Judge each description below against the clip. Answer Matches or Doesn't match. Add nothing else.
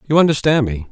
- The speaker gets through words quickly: Doesn't match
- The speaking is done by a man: Matches